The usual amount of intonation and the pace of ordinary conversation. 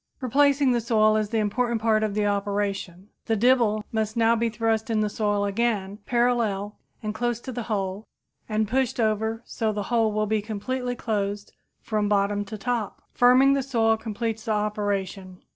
No: narrow, 2.3 semitones; average, 185 wpm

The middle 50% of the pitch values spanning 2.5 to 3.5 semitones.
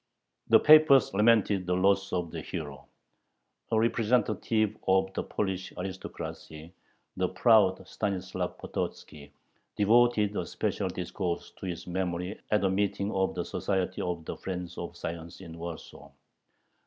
Yes: average, 2.9 semitones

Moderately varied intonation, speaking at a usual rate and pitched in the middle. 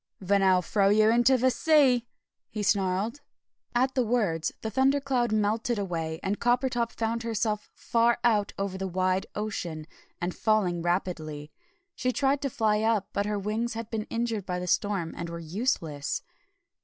No: average, 4.3 semitones; average, 165 wpm; high, 215 Hz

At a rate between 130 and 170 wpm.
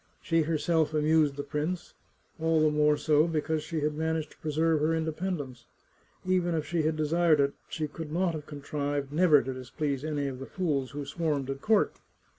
No: average, 190 wpm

